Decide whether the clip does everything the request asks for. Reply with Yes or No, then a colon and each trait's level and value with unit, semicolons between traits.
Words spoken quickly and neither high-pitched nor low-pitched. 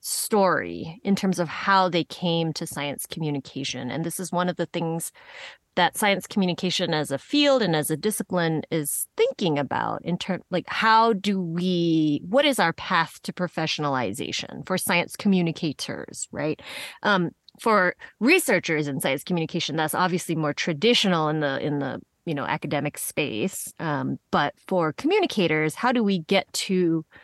No: average, 160 wpm; medium, 175 Hz